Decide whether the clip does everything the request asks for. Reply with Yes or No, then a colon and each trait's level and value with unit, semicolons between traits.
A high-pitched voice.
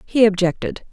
Yes: high, 210 Hz